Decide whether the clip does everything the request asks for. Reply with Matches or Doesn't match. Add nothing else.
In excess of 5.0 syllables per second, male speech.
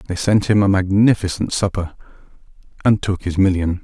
Matches